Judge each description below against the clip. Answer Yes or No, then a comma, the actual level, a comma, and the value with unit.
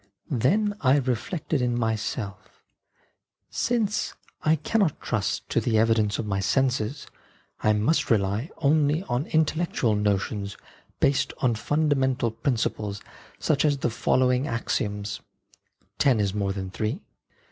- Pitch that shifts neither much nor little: No, wide, 5.7 semitones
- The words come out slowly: Yes, slow, 130 wpm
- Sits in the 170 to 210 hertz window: No, low, 125 Hz